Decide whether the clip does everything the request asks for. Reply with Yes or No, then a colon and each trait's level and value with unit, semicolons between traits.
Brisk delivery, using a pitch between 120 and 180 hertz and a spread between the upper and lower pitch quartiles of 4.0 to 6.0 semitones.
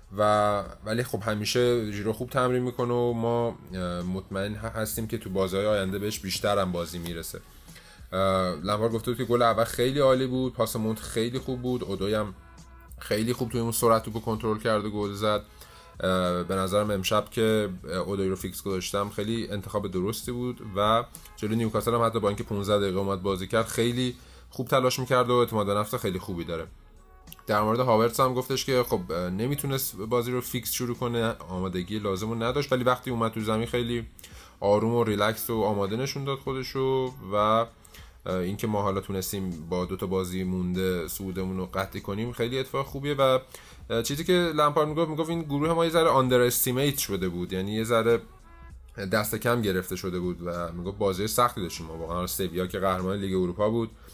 No: fast, 180 wpm; low, 110 Hz; average, 4.3 semitones